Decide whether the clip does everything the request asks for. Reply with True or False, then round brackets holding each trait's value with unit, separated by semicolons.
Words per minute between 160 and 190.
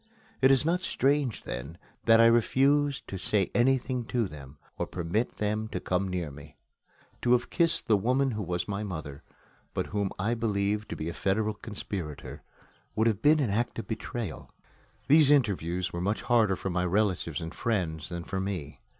True (185 wpm)